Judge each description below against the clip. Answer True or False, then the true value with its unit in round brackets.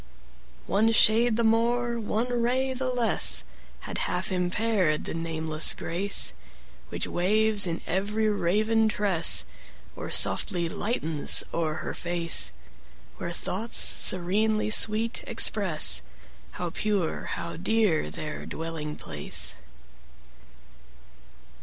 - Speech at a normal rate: False (110 wpm)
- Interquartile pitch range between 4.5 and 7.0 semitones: True (4.8 semitones)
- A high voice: True (205 Hz)